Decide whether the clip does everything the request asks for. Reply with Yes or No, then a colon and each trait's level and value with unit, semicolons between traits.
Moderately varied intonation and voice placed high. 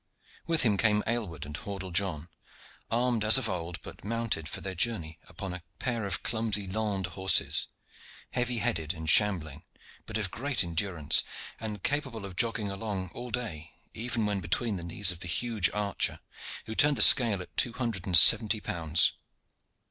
No: average, 4.5 semitones; low, 100 Hz